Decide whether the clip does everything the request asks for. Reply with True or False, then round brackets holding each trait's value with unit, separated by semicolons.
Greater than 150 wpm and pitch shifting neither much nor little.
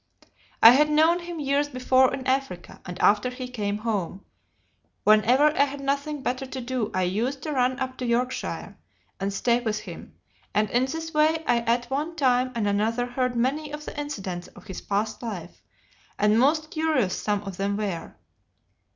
True (180 wpm; 4.9 semitones)